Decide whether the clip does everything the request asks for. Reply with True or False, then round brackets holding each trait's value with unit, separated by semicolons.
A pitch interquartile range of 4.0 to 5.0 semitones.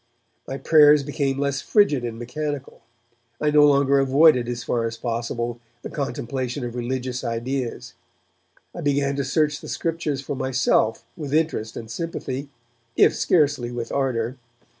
False (3.4 semitones)